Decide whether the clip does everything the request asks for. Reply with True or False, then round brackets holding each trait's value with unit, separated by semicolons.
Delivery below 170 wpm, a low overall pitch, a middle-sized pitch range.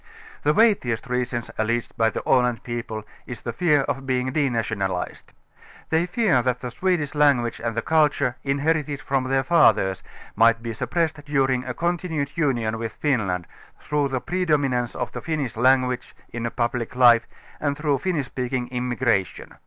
True (160 wpm; 130 Hz; 3.8 semitones)